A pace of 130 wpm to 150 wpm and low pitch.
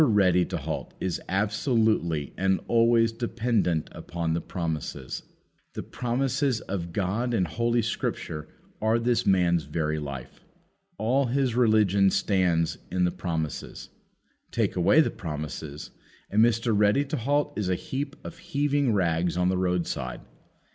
Yes: average, 140 wpm; low, 100 Hz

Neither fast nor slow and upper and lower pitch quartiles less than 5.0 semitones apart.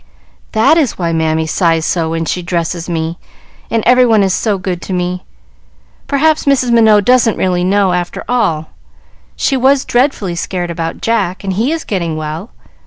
No: average, 175 wpm; wide, 5.5 semitones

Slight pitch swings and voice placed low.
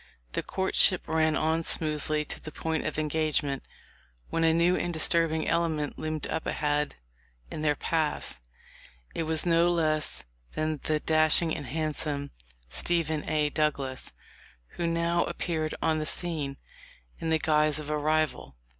No: narrow, 1.3 semitones; medium, 155 Hz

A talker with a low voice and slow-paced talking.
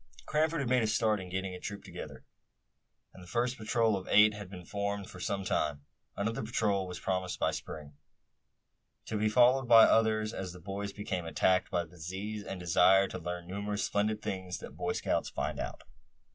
No: low, 100 Hz; average, 200 wpm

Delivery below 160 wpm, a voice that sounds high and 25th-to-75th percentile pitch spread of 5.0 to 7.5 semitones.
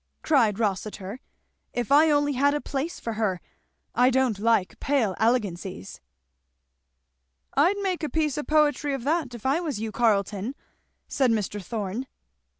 Yes: average, 150 wpm; high, 245 Hz; wide, 5.5 semitones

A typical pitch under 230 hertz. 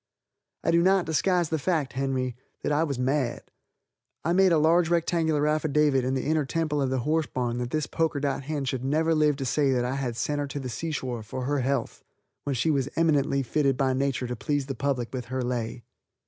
Yes: medium, 140 Hz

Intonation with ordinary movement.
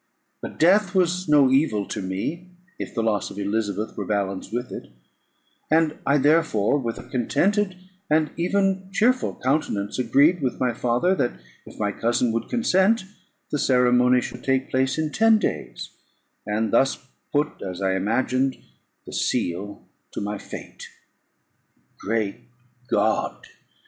No: wide, 7.2 semitones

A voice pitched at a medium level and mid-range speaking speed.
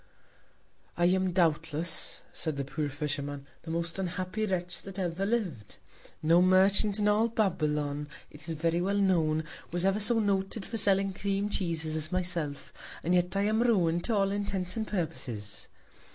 Yes: medium, 180 Hz; average, 165 wpm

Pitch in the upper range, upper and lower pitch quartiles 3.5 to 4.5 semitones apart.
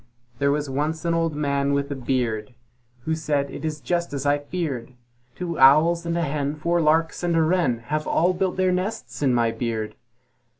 No: medium, 150 Hz; average, 3.8 semitones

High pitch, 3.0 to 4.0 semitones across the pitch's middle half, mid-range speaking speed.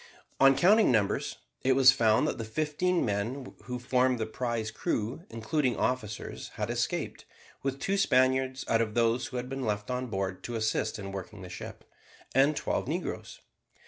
No: low, 125 Hz; average, 3.4 semitones; average, 175 wpm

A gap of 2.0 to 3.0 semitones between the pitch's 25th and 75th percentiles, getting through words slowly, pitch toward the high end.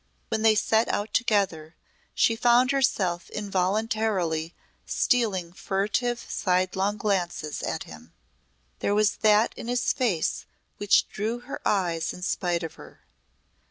No: average, 3.9 semitones; slow, 125 wpm; high, 205 Hz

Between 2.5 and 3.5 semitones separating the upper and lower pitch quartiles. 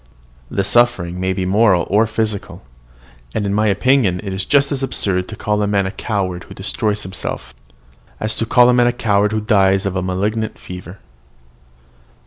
Yes: average, 2.8 semitones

